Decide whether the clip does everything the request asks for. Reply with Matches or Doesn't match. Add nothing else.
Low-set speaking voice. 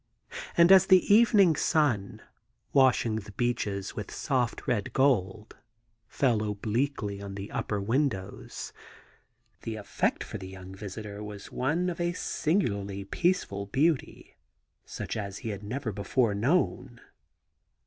Matches